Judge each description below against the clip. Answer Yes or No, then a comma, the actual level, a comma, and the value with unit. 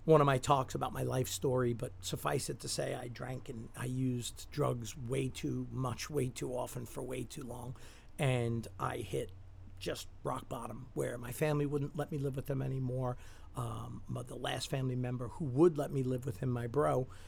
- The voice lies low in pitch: Yes, low, 125 Hz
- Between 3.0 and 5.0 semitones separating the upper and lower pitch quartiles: No, narrow, 2.4 semitones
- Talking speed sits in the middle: No, fast, 210 wpm